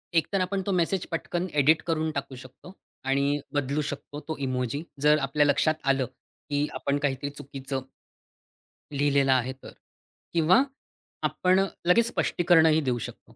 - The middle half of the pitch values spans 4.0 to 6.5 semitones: No, average, 3.2 semitones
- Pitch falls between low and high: Yes, medium, 145 Hz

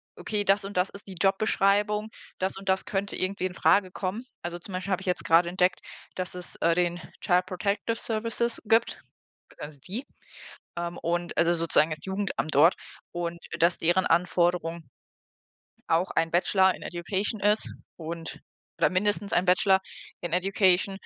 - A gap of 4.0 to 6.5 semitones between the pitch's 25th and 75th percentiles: No, narrow, 2.5 semitones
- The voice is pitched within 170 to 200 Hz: Yes, medium, 185 Hz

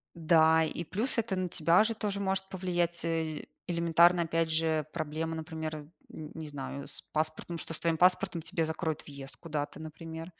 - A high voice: No, medium, 165 Hz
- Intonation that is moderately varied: No, narrow, 1.8 semitones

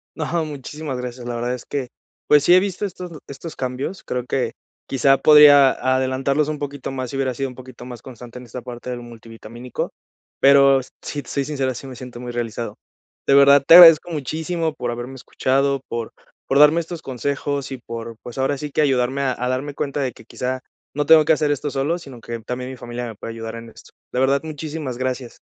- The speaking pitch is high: No, low, 135 Hz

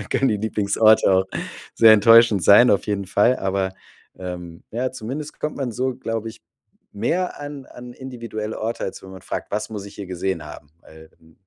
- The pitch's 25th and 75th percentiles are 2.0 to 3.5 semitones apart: No, average, 4.3 semitones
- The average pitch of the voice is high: No, low, 110 Hz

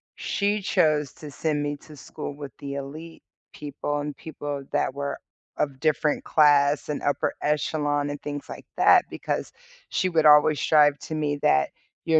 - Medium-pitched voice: Yes, medium, 145 Hz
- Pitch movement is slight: Yes, narrow, 1.3 semitones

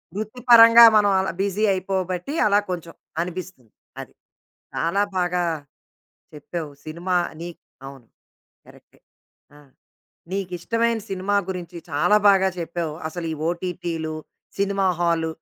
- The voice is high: No, medium, 180 Hz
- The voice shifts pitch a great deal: No, average, 2.9 semitones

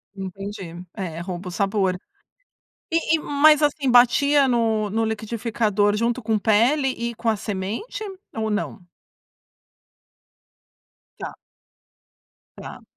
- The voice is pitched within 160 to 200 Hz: No, high, 220 Hz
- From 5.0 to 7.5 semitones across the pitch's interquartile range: No, average, 3.7 semitones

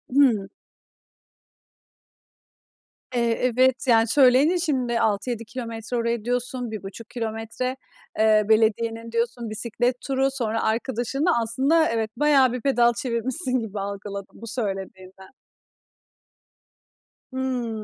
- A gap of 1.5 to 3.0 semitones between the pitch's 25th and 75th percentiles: Yes, average, 2.7 semitones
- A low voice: No, high, 235 Hz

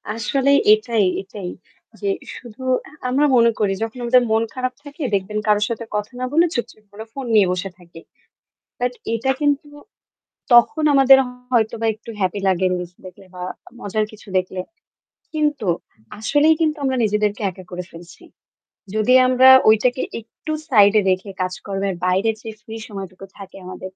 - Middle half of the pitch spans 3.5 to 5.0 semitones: Yes, average, 4.6 semitones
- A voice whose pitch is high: Yes, high, 215 Hz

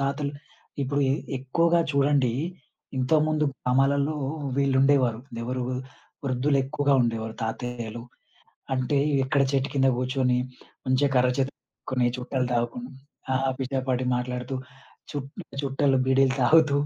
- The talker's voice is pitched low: Yes, low, 130 Hz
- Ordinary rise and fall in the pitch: No, narrow, 1.9 semitones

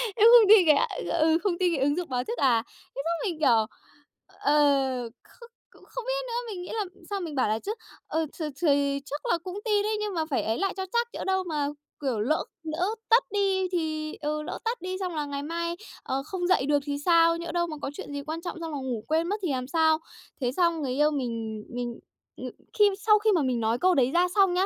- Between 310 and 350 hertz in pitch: Yes, very high, 320 Hz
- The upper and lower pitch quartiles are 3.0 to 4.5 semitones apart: No, average, 4.9 semitones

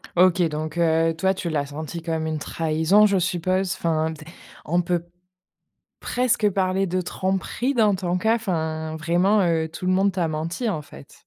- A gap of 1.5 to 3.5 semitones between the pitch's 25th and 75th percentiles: Yes, average, 3.1 semitones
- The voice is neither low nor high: Yes, medium, 175 Hz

